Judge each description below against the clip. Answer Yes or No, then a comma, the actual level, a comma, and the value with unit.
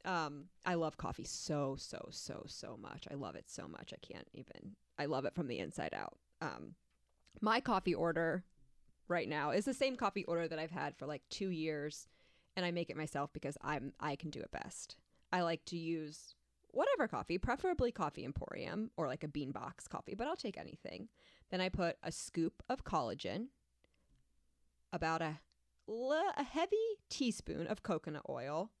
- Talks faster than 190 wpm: No, average, 185 wpm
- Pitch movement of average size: Yes, average, 4.2 semitones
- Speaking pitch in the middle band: Yes, medium, 165 Hz